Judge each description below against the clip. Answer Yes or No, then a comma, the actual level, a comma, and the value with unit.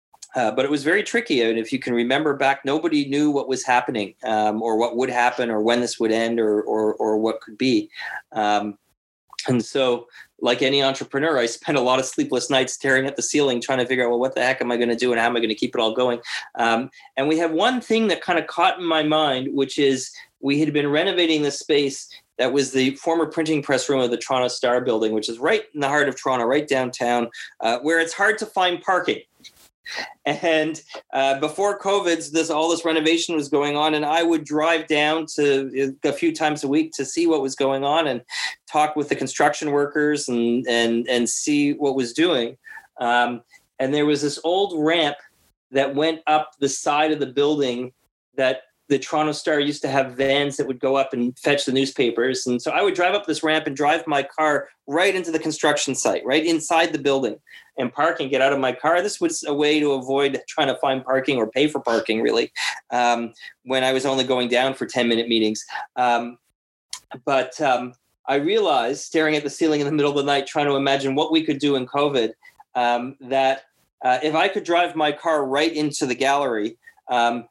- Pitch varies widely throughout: No, average, 3.7 semitones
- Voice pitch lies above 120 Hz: Yes, medium, 140 Hz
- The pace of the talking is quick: Yes, fast, 225 wpm